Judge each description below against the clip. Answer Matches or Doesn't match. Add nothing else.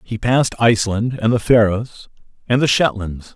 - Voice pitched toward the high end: Doesn't match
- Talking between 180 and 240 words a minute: Doesn't match